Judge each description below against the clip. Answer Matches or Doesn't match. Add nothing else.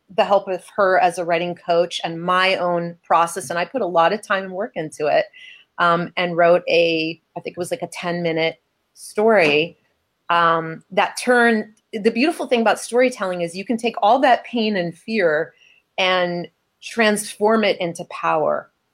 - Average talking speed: Matches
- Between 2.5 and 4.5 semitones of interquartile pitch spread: Matches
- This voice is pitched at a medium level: Matches